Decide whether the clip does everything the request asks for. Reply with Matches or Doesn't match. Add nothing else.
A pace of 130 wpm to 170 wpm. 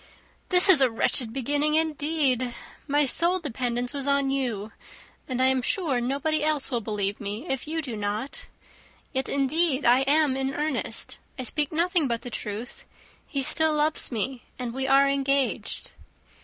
Matches